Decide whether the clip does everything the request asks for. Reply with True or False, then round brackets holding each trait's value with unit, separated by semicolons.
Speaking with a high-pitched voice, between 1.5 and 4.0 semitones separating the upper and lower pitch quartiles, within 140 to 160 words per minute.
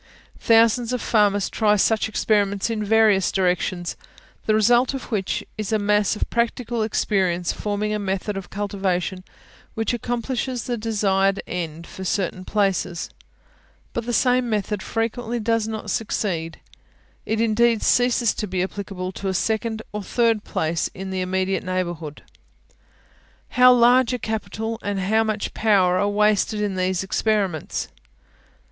True (210 Hz; 2.9 semitones; 145 wpm)